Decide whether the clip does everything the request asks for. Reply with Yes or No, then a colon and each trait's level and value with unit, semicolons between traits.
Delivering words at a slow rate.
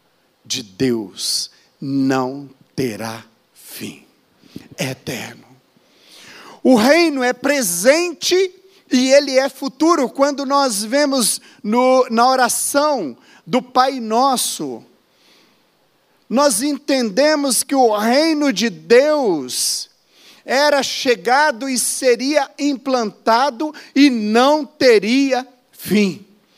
Yes: slow, 90 wpm